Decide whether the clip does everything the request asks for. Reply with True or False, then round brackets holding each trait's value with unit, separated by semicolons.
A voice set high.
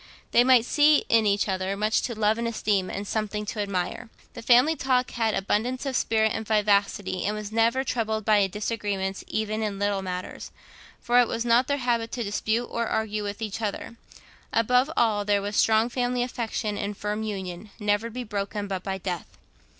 True (215 Hz)